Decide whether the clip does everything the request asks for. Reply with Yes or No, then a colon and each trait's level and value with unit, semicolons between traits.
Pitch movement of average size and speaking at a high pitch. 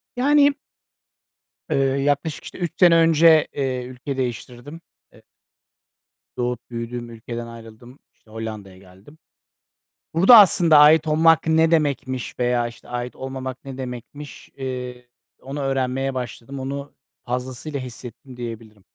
No: average, 3.6 semitones; low, 130 Hz